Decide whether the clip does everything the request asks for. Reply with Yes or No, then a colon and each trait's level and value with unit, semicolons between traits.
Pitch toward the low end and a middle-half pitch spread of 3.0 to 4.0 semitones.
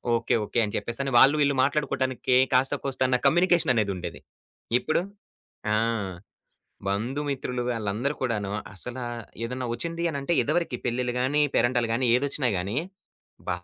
Yes: low, 125 Hz; average, 3.3 semitones